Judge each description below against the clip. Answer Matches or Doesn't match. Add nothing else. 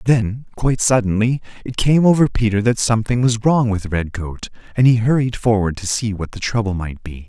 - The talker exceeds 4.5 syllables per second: Matches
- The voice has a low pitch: Matches